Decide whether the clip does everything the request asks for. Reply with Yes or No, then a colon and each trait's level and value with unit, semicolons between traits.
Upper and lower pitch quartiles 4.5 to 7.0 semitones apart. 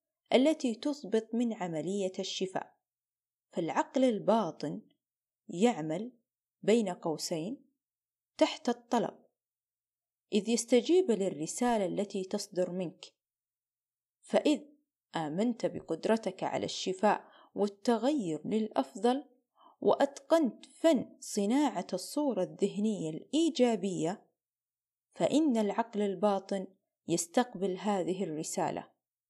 Yes: average, 5.2 semitones